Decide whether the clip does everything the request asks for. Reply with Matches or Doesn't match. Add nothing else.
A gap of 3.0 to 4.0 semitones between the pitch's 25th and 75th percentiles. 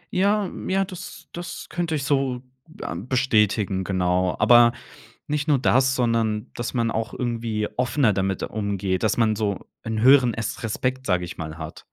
Doesn't match